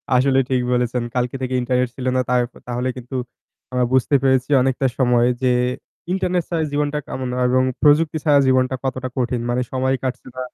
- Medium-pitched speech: No, low, 130 Hz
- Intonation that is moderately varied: No, narrow, 1.4 semitones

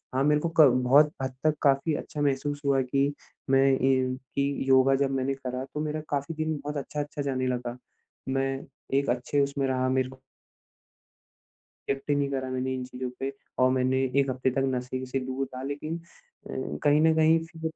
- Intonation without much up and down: Yes, narrow, 2.0 semitones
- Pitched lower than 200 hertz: Yes, low, 135 Hz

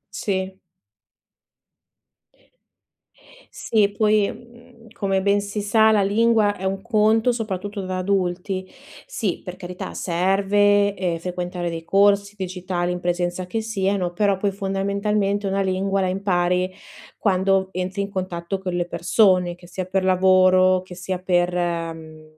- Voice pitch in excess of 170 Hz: Yes, high, 190 Hz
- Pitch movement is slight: Yes, narrow, 1.9 semitones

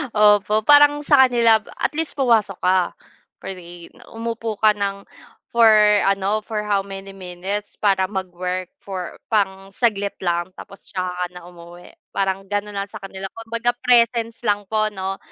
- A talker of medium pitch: No, high, 200 Hz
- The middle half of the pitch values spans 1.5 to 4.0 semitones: Yes, average, 2.9 semitones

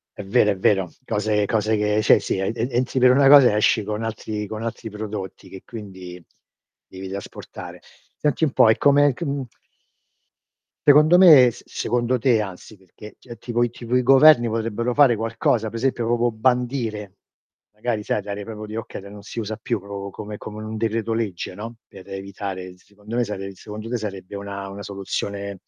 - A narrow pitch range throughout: No, average, 3.0 semitones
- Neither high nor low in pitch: No, low, 110 Hz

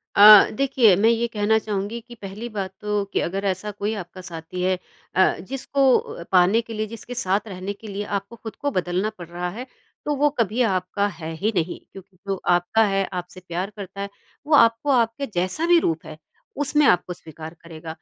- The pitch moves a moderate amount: Yes, average, 3.9 semitones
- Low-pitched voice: No, high, 200 Hz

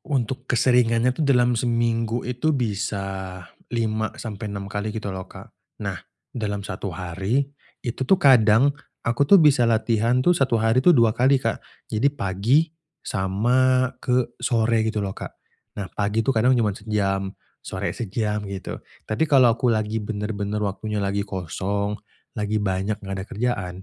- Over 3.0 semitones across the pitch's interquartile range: Yes, average, 3.4 semitones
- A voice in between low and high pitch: No, low, 110 Hz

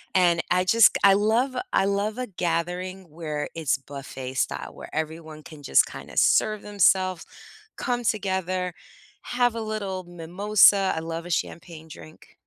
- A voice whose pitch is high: No, medium, 180 Hz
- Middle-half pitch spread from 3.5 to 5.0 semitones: Yes, average, 4.0 semitones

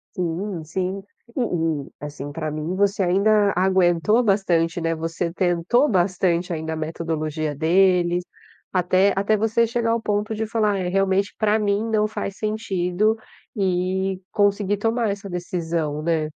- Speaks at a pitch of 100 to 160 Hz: No, medium, 185 Hz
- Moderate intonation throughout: Yes, average, 3.6 semitones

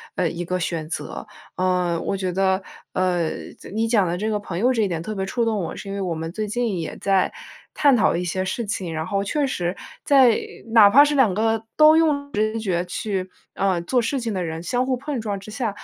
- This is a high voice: Yes, high, 200 Hz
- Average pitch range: Yes, average, 4.6 semitones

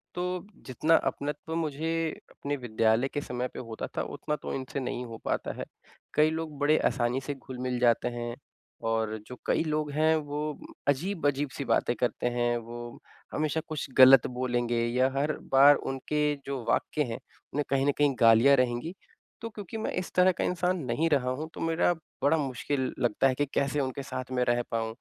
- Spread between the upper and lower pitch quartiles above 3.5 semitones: Yes, average, 3.9 semitones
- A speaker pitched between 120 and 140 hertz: Yes, low, 135 Hz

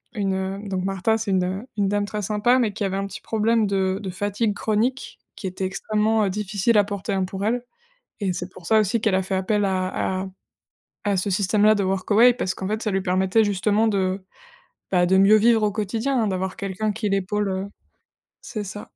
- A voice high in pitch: Yes, high, 200 Hz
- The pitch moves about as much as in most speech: No, narrow, 2.2 semitones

